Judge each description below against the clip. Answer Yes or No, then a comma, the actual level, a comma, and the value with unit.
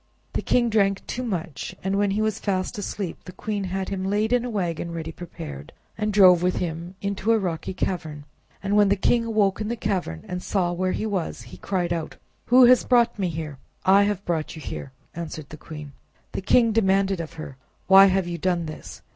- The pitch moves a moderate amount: Yes, average, 3.5 semitones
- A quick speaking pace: Yes, fast, 215 wpm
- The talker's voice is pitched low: No, high, 190 Hz